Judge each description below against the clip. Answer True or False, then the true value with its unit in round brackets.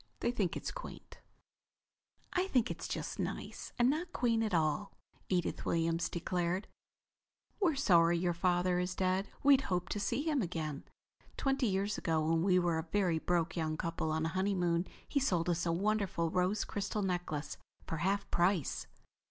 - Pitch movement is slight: False (3.7 semitones)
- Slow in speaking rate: False (170 wpm)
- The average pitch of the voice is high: False (180 Hz)